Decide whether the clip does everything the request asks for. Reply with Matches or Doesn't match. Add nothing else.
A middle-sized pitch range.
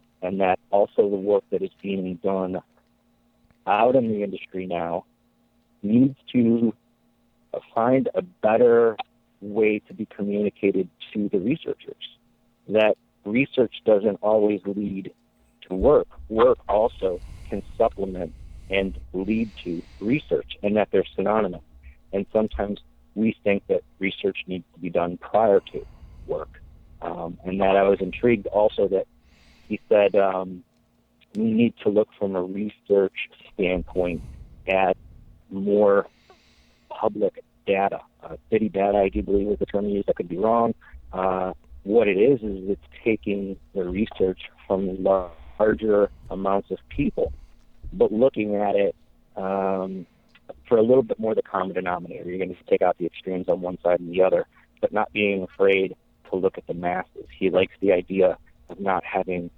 Matches